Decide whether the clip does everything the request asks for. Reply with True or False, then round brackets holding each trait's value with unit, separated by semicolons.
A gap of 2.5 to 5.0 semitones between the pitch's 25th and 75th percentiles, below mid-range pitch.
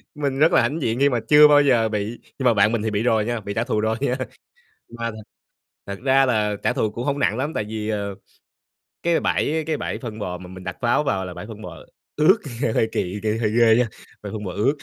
True (4.4 semitones; 115 Hz)